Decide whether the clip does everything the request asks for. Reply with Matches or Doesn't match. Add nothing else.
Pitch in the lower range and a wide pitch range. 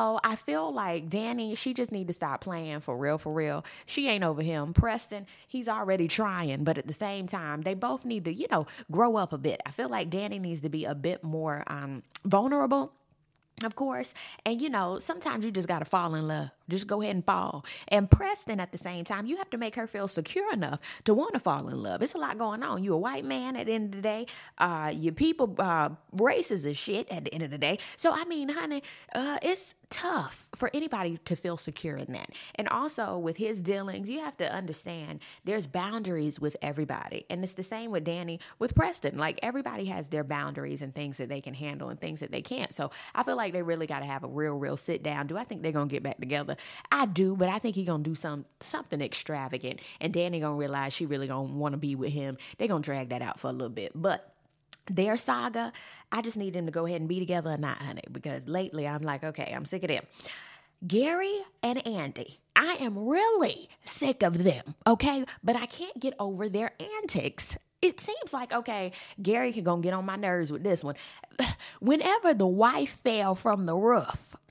Doesn't match